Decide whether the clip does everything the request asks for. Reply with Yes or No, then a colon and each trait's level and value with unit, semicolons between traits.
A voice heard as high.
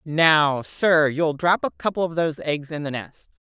No: medium, 155 Hz